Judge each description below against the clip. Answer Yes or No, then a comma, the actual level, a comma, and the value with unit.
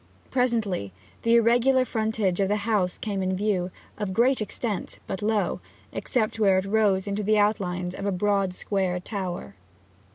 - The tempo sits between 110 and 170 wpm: Yes, average, 160 wpm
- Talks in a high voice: Yes, high, 205 Hz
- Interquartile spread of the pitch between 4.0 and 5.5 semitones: No, average, 2.7 semitones